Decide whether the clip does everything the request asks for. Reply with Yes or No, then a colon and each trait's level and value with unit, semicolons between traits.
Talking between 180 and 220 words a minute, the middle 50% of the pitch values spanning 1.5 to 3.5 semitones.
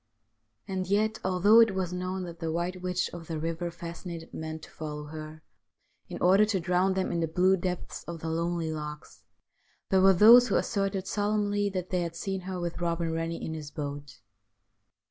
Yes: average, 190 wpm; narrow, 2.6 semitones